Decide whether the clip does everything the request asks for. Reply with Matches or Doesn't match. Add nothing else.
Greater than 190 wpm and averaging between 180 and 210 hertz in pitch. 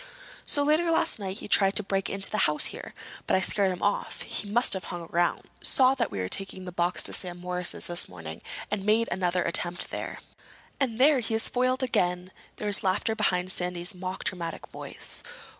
Matches